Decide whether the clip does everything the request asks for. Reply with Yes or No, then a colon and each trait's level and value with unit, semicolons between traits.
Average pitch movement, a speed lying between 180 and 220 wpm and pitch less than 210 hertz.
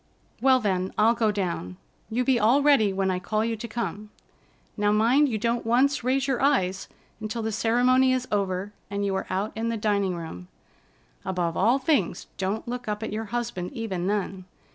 No: average, 3.8 semitones; average, 190 wpm; high, 215 Hz